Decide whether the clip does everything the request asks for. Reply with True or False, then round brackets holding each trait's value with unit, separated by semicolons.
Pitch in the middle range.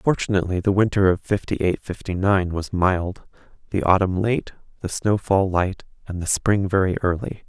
False (95 Hz)